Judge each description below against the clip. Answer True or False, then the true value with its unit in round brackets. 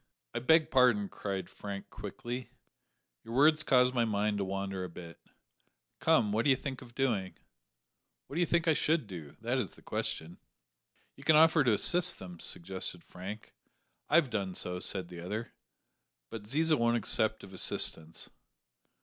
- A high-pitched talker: False (110 Hz)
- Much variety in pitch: True (6.0 semitones)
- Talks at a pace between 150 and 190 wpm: True (165 wpm)